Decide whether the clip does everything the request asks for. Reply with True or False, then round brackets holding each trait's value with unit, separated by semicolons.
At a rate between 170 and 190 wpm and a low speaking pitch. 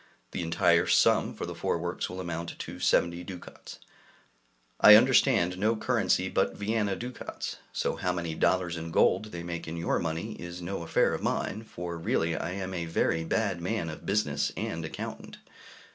True (175 wpm; 85 Hz)